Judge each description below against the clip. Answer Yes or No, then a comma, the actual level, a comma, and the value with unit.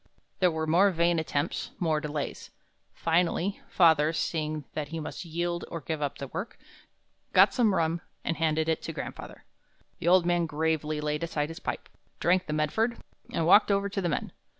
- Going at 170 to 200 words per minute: Yes, average, 180 wpm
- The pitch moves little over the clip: Yes, narrow, 2.2 semitones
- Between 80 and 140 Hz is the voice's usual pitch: No, medium, 165 Hz